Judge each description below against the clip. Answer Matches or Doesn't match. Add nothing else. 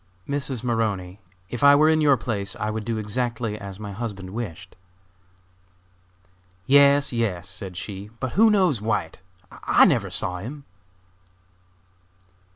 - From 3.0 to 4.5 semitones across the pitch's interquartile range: Doesn't match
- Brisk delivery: Doesn't match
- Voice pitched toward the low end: Matches